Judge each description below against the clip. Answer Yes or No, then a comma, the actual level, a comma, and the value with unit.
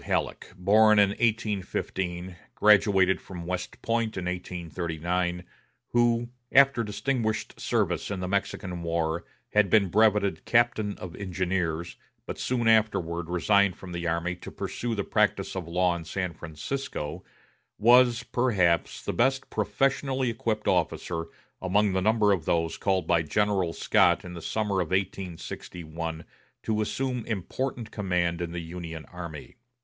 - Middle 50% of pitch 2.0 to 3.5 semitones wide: No, average, 4.1 semitones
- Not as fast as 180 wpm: Yes, average, 140 wpm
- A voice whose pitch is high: No, very low, 95 Hz